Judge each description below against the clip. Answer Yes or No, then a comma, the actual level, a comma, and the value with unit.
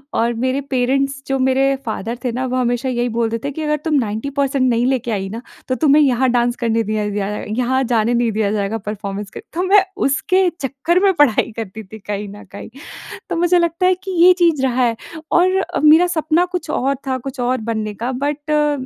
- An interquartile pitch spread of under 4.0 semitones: No, average, 4.6 semitones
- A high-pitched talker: Yes, very high, 255 Hz